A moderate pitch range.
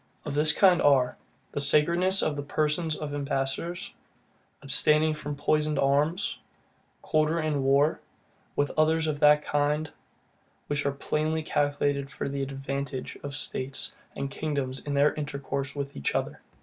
No: narrow, 1.8 semitones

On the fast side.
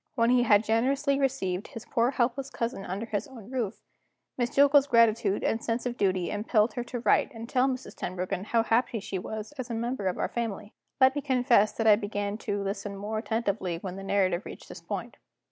Yes: fast, 210 wpm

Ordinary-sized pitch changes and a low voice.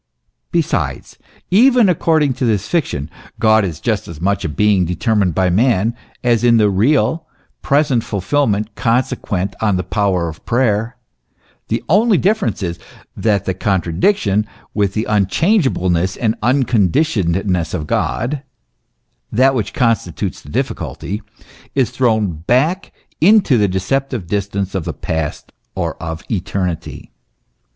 No: wide, 5.8 semitones; low, 105 Hz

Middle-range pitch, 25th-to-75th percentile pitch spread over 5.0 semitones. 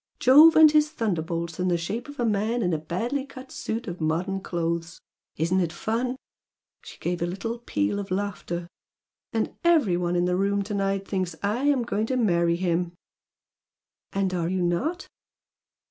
No: high, 195 Hz; wide, 5.4 semitones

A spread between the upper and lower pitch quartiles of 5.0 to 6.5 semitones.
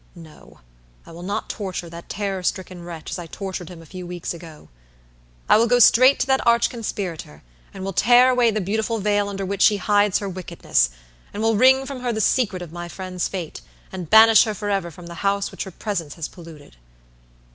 No: average, 4.0 semitones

